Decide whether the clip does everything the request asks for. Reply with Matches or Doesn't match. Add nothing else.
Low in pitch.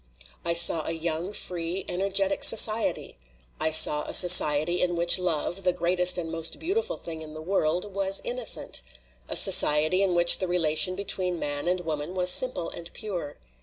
Doesn't match